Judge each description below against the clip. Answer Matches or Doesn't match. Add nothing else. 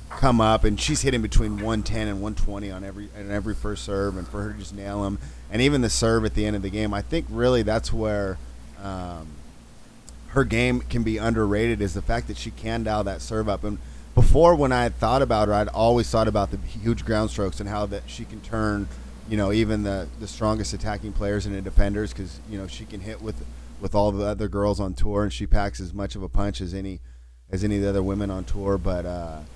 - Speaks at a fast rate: Matches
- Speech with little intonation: Matches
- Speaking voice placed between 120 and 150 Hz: Doesn't match